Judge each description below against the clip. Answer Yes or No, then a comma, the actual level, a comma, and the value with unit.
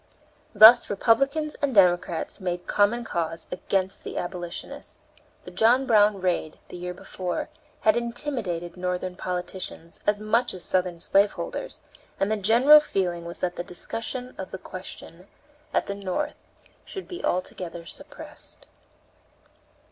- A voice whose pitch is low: No, high, 190 Hz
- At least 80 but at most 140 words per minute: Yes, slow, 135 wpm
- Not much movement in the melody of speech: No, average, 4.2 semitones